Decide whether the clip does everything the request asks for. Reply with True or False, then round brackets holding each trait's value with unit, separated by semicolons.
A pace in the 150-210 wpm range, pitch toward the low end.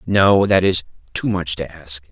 True (200 wpm; 90 Hz)